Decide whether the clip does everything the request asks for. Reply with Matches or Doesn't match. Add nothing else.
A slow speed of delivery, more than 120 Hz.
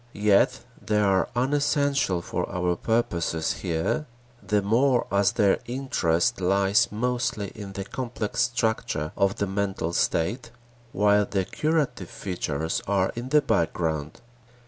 Doesn't match